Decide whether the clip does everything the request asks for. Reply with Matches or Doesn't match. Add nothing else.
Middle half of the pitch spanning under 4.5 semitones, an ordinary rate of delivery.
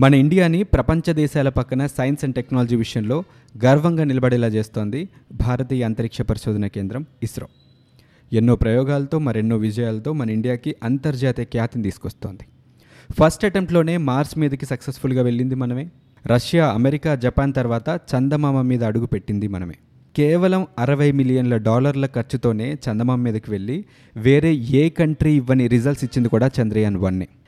Doesn't match